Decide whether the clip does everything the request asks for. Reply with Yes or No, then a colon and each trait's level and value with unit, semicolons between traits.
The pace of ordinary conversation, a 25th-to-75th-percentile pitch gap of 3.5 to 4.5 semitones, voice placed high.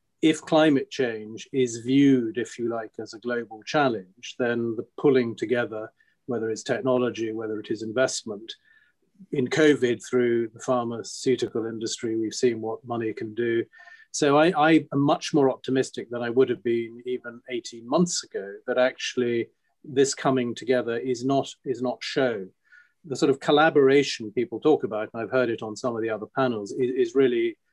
No: average, 175 wpm; average, 4.2 semitones; low, 125 Hz